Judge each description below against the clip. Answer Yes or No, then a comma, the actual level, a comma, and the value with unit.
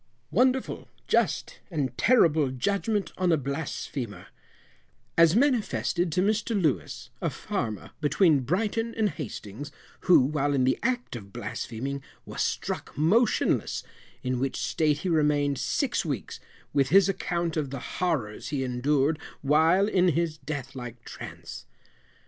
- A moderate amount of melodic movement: No, wide, 5.8 semitones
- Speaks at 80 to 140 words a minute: Yes, slow, 135 wpm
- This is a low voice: No, medium, 155 Hz